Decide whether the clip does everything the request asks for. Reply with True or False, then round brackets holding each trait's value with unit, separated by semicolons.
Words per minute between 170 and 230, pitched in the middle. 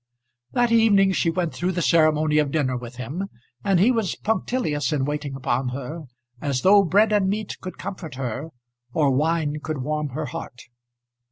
True (175 wpm; 155 Hz)